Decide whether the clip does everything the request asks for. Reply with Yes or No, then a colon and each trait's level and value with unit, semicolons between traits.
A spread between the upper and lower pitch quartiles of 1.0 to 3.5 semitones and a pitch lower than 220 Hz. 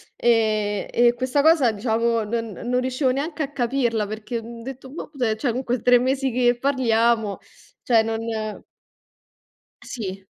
No: narrow, 2.6 semitones; high, 240 Hz